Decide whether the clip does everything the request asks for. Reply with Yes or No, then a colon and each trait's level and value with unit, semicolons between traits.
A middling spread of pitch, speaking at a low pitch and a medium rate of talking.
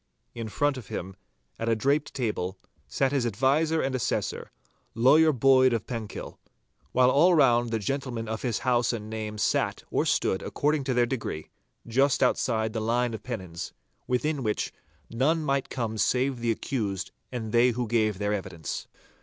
Yes: average, 3.5 semitones; low, 120 Hz; average, 170 wpm